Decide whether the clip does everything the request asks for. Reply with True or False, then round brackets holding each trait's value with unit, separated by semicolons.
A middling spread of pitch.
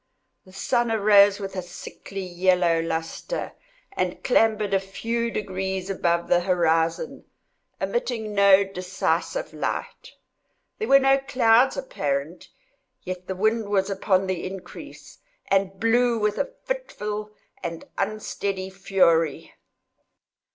True (3.5 semitones)